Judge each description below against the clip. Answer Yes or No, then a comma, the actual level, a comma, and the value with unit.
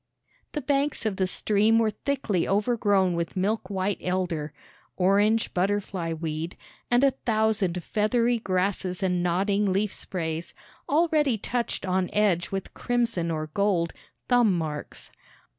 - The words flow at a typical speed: No, slow, 130 wpm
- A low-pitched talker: No, high, 195 Hz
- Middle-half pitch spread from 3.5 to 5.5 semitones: Yes, average, 3.8 semitones